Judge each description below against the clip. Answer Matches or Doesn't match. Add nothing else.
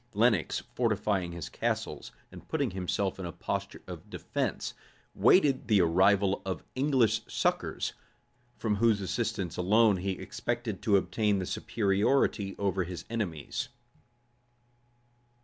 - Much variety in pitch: Doesn't match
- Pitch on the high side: Doesn't match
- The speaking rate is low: Matches